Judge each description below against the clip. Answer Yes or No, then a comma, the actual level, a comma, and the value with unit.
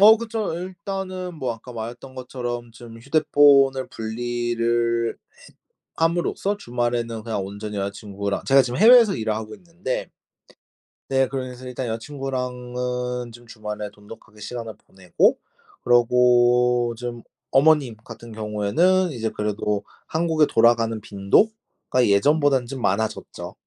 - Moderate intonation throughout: Yes, average, 3.7 semitones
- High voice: No, low, 120 Hz